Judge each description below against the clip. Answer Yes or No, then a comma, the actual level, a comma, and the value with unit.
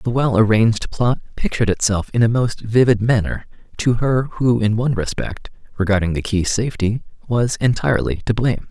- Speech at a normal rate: Yes, average, 170 wpm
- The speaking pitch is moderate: No, low, 110 Hz